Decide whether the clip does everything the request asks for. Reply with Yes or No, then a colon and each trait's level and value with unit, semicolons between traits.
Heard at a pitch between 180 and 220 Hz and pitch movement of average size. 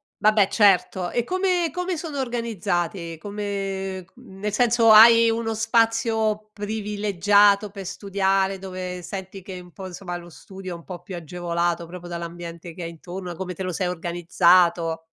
Yes: high, 190 Hz; average, 3.4 semitones